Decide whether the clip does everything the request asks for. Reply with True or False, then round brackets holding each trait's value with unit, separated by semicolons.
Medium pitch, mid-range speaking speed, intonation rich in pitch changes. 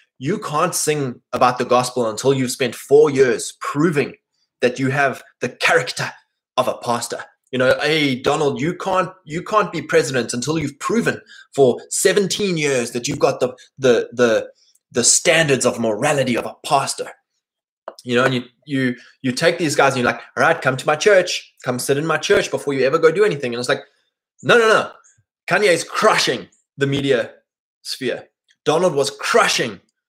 True (145 Hz; 185 wpm; 6.9 semitones)